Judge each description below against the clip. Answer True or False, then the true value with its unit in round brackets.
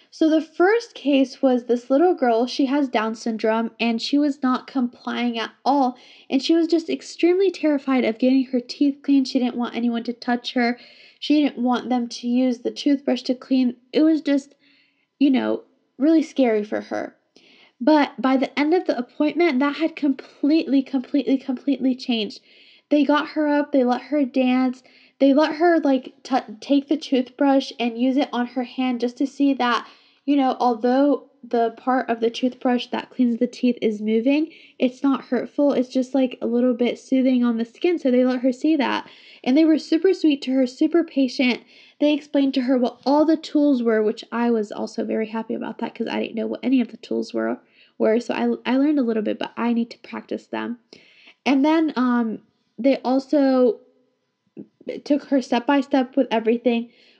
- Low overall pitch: False (260 Hz)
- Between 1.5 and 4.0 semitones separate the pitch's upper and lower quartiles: True (3.0 semitones)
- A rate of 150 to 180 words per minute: False (200 wpm)